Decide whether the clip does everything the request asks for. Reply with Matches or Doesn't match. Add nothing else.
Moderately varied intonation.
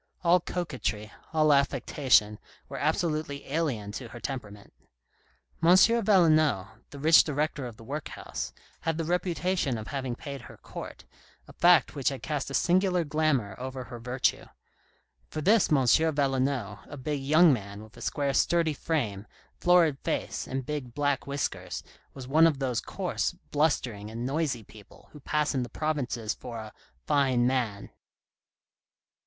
Matches